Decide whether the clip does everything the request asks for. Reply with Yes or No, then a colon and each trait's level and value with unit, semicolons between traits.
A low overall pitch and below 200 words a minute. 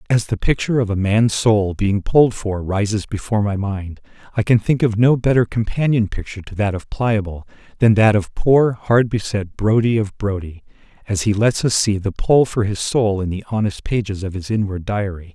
No: low, 105 Hz; fast, 205 wpm